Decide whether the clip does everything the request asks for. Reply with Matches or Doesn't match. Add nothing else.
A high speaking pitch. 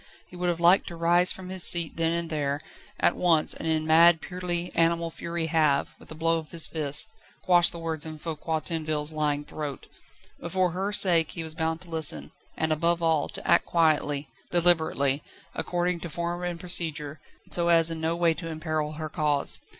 Doesn't match